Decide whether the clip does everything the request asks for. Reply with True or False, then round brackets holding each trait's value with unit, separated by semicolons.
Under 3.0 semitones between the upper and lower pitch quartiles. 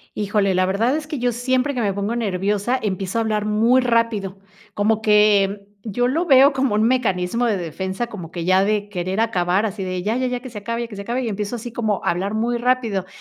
False (3.5 semitones)